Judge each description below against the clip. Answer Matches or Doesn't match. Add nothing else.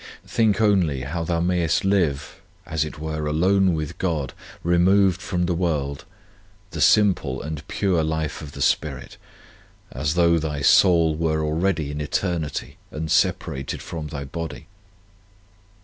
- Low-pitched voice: Matches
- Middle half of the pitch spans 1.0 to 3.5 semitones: Matches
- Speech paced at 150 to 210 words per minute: Doesn't match